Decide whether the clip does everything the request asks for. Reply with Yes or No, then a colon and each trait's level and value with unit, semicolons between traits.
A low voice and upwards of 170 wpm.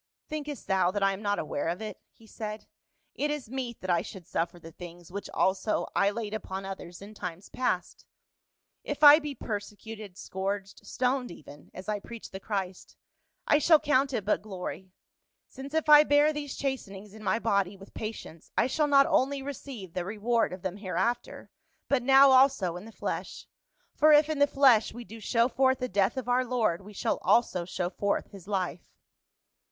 No: high, 215 Hz; average, 200 wpm